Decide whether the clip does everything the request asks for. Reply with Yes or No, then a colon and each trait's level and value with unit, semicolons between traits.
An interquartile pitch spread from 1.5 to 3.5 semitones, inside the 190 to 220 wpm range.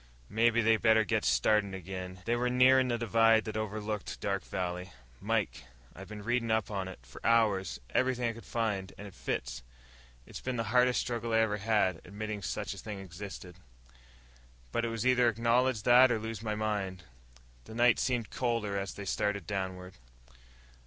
No: average, 3.2 semitones; average, 180 wpm